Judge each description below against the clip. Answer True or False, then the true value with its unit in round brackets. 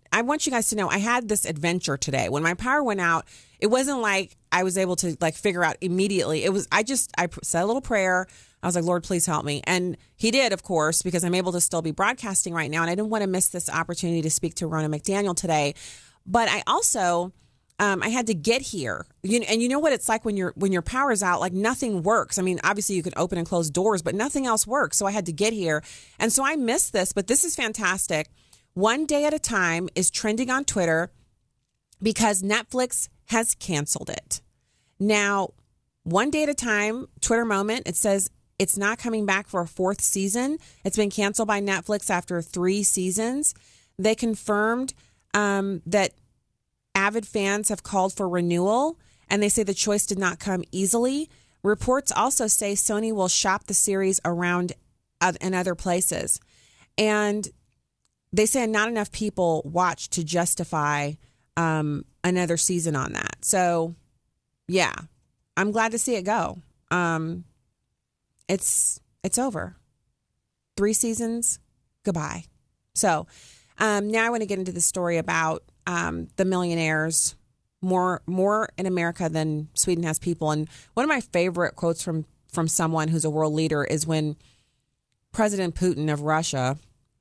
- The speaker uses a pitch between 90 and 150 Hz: False (185 Hz)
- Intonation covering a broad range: False (4.3 semitones)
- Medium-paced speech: True (180 wpm)